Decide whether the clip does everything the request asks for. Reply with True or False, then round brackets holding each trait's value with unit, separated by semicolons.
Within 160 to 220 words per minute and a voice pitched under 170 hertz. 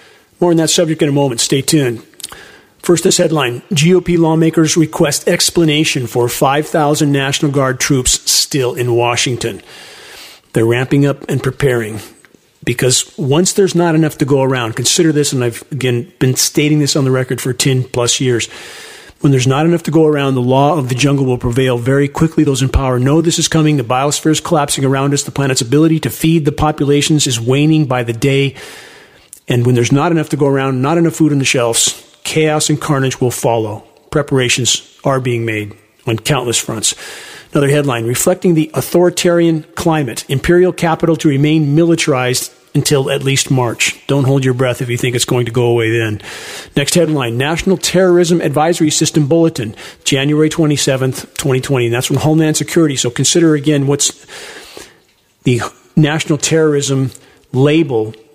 True (175 wpm; 140 Hz)